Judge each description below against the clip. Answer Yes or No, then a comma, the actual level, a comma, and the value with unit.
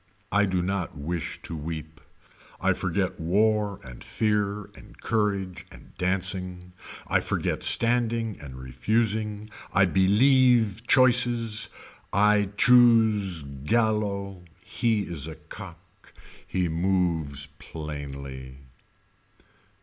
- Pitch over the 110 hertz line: No, very low, 95 Hz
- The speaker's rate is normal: No, slow, 100 wpm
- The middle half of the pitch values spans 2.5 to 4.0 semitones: No, average, 4.7 semitones